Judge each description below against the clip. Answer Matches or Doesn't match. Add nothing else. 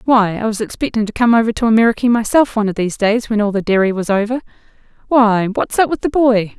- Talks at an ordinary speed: Doesn't match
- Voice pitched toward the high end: Matches